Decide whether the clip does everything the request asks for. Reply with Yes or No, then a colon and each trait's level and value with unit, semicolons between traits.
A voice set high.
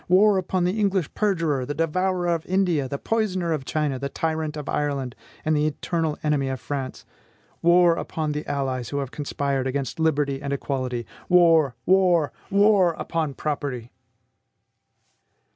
No: medium, 155 Hz